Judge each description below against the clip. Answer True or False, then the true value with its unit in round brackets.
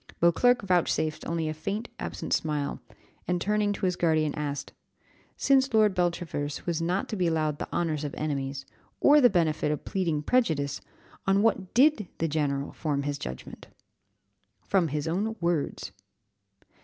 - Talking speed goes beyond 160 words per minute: False (155 wpm)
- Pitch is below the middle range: False (165 Hz)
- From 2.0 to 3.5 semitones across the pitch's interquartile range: False (4.7 semitones)